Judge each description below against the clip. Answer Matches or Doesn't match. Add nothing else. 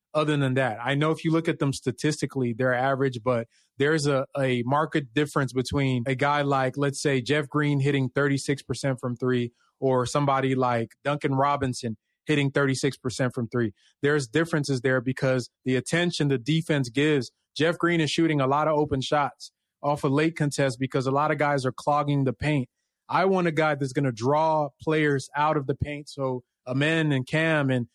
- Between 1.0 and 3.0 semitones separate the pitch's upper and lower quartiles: Matches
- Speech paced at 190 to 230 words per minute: Matches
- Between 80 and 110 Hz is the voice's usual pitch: Doesn't match